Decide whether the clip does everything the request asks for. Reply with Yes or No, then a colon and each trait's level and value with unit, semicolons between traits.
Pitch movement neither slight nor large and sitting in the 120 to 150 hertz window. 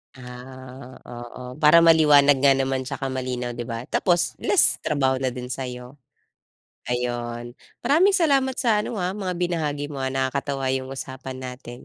Yes: average, 3.9 semitones; low, 135 Hz